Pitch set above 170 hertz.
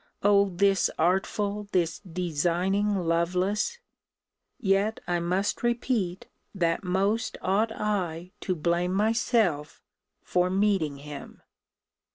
Yes: high, 190 Hz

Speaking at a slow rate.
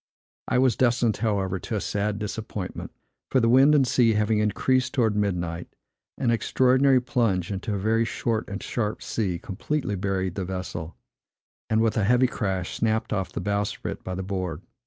No: average, 175 wpm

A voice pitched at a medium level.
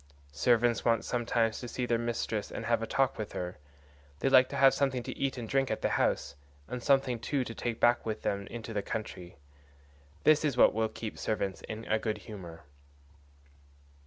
No: low, 115 Hz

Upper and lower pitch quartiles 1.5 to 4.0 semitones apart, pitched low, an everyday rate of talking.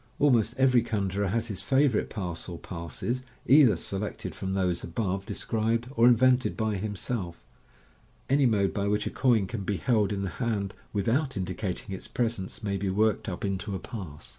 Yes: average, 3.5 semitones; low, 105 Hz; average, 160 wpm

